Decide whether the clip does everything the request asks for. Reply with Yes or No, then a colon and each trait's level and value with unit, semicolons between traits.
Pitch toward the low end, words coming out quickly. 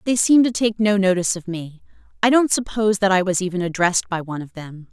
No: high, 195 Hz; fast, 245 wpm